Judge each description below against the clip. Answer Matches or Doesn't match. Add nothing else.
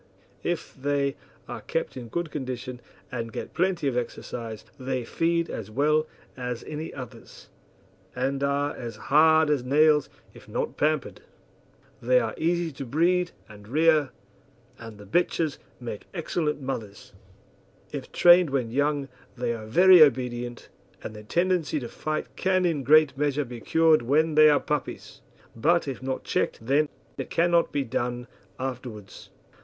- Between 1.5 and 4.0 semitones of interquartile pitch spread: Doesn't match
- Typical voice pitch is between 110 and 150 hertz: Matches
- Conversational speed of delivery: Matches